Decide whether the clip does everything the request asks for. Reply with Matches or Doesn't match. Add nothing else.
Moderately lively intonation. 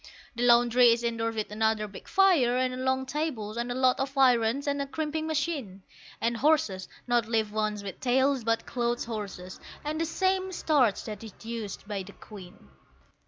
Matches